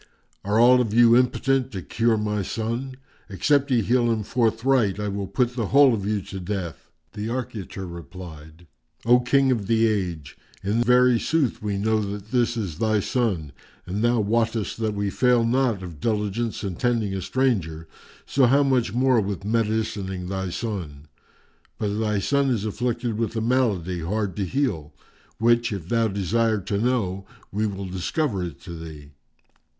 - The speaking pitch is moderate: No, low, 110 Hz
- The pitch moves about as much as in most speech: Yes, average, 3.8 semitones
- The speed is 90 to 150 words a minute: No, average, 170 wpm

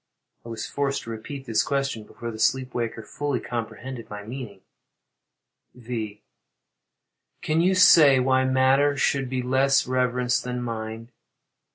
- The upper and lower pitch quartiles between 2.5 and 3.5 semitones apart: Yes, average, 2.9 semitones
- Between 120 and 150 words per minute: Yes, average, 140 wpm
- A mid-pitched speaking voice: No, low, 125 Hz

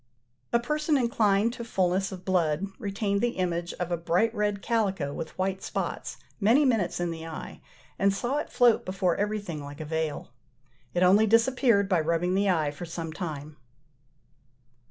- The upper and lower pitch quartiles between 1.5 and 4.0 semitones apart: No, average, 4.5 semitones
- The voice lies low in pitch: No, high, 190 Hz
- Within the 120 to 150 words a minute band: No, average, 170 wpm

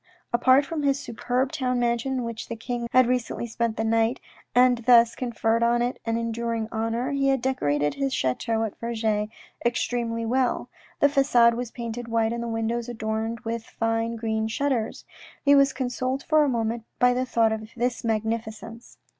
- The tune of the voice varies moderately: No, narrow, 1.9 semitones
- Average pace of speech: Yes, average, 180 wpm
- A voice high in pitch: Yes, high, 235 Hz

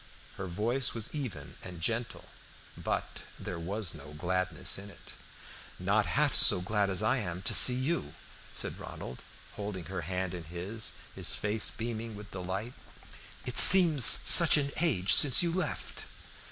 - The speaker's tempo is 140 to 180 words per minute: Yes, average, 155 wpm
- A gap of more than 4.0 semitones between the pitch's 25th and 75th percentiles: Yes, average, 5.0 semitones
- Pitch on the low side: Yes, low, 100 Hz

